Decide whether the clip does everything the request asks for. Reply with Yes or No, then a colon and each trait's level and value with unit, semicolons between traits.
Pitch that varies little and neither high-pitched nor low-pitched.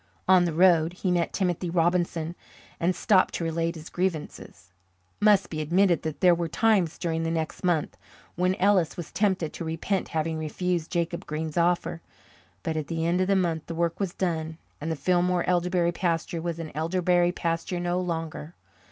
Yes: narrow, 1.9 semitones; medium, 170 Hz